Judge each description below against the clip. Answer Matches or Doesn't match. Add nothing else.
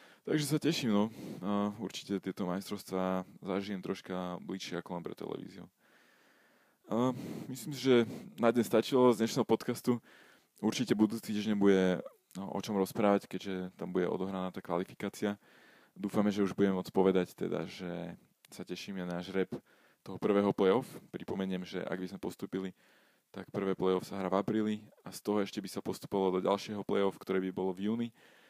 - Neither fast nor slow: Doesn't match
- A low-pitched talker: Matches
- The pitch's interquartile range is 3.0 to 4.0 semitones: Doesn't match